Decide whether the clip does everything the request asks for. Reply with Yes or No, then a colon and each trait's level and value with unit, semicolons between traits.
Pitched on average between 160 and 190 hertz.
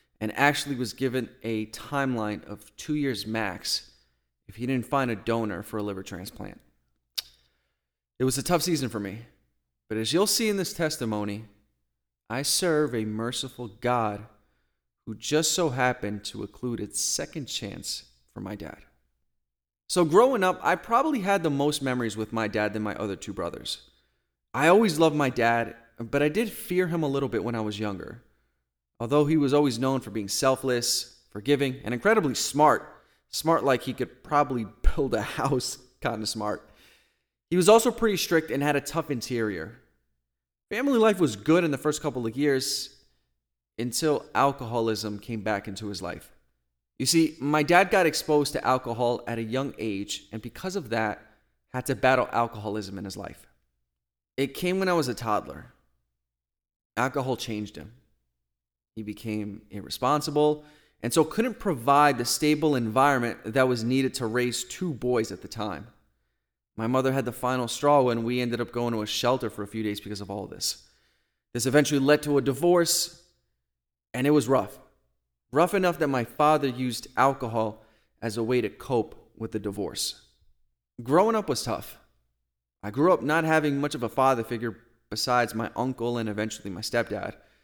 No: low, 120 Hz